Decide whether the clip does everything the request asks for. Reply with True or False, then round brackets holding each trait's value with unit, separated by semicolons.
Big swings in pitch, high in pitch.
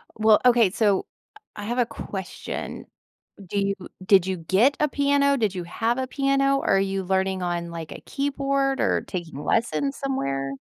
True (6.5 semitones; 215 Hz)